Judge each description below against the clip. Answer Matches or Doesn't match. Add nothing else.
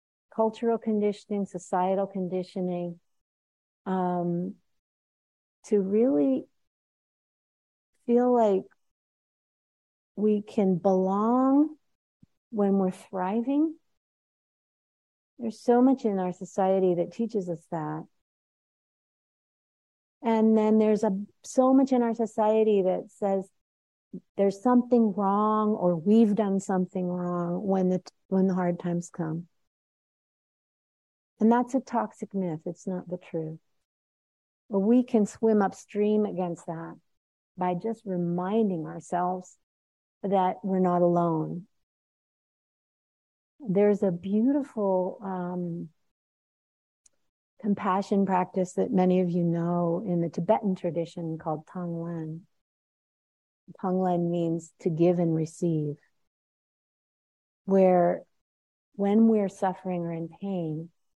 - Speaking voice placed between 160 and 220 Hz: Matches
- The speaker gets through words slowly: Matches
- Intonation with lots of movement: Doesn't match